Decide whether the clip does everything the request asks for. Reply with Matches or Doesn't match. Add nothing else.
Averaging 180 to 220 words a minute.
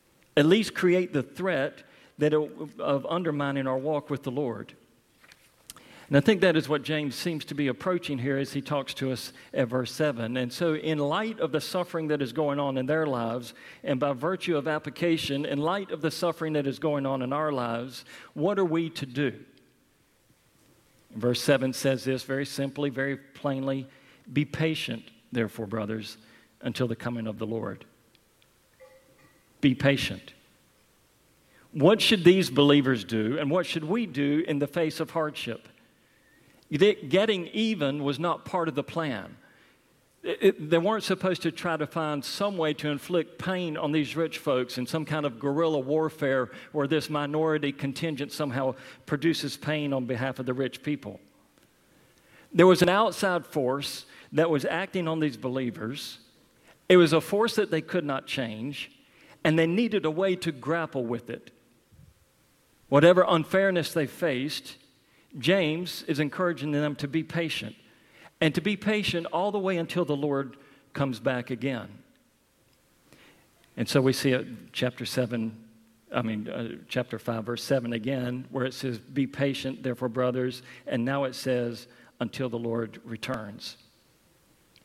Doesn't match